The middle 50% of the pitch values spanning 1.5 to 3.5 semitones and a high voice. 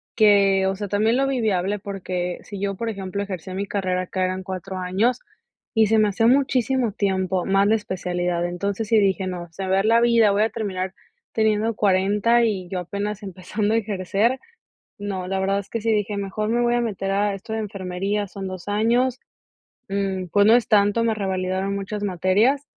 Yes: narrow, 2.6 semitones; high, 200 Hz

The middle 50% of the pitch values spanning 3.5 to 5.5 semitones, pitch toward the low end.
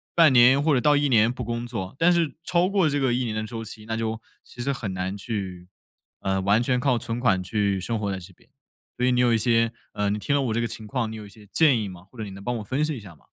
Yes: average, 3.8 semitones; low, 115 Hz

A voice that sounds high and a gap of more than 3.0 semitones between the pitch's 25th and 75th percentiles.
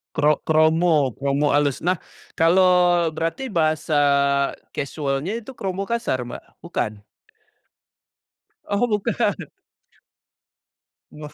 No: medium, 160 Hz; average, 3.8 semitones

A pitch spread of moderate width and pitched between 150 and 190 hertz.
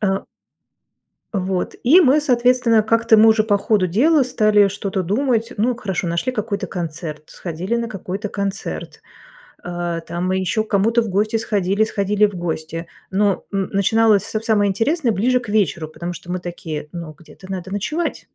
No: average, 3.8 semitones; high, 205 Hz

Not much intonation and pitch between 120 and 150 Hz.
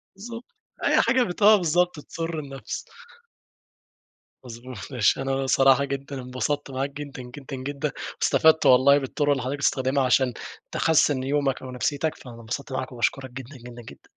Yes: narrow, 2.2 semitones; low, 135 Hz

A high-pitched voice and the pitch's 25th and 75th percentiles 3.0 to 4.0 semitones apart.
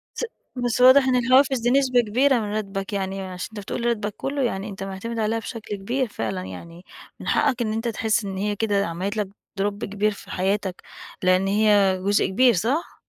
Yes: high, 210 Hz; average, 3.6 semitones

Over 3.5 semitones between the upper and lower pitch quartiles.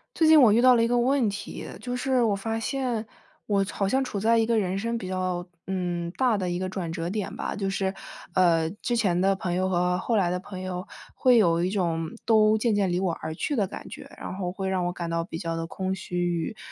Yes: average, 4.1 semitones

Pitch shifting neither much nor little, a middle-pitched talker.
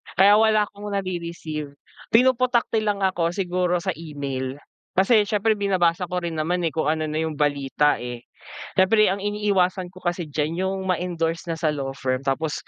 Yes: average, 4.4 semitones; medium, 175 Hz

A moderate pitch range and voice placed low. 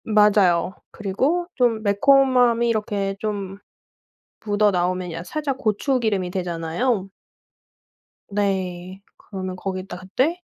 No: average, 4.0 semitones; high, 200 Hz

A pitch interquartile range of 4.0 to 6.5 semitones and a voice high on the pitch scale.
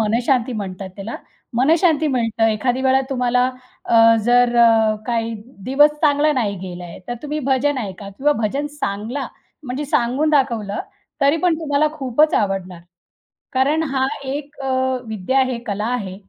Yes: average, 4.5 semitones; very high, 250 Hz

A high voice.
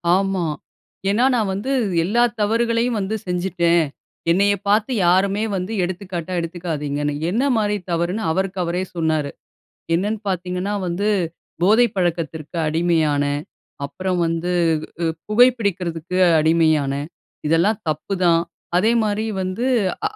No: medium, 180 Hz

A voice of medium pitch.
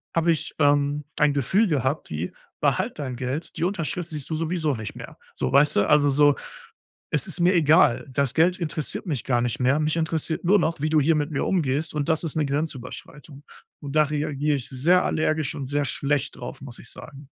Yes: medium, 150 Hz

